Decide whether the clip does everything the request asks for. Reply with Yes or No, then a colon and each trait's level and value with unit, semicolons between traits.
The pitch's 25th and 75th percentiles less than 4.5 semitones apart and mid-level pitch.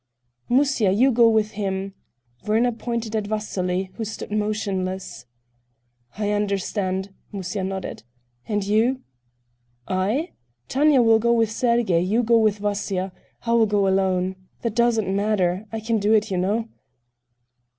No: average, 2.9 semitones; high, 210 Hz